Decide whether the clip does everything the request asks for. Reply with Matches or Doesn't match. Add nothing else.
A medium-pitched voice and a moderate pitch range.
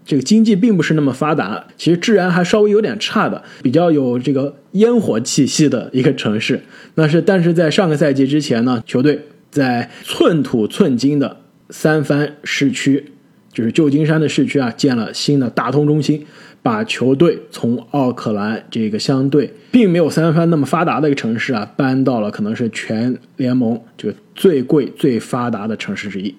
Matches